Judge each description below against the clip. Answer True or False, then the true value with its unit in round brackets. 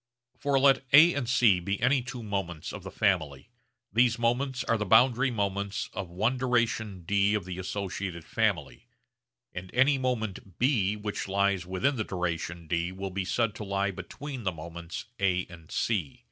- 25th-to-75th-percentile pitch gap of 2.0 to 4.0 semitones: False (4.8 semitones)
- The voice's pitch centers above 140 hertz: False (100 Hz)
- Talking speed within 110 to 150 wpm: False (175 wpm)